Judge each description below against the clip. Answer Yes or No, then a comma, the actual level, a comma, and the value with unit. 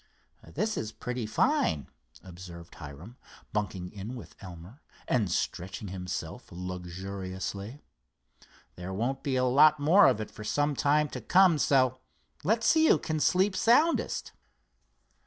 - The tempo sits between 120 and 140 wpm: Yes, slow, 135 wpm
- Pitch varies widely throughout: Yes, wide, 8.0 semitones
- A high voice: No, low, 110 Hz